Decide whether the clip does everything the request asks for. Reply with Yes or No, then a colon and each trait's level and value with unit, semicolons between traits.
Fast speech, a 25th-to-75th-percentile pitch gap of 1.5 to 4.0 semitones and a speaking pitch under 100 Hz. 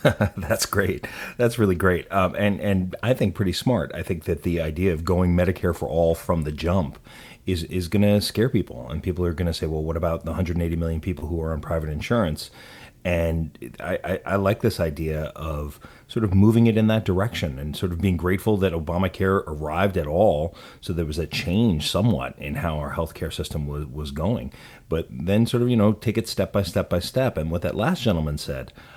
Yes: fast, 220 wpm; average, 3.7 semitones; very low, 90 Hz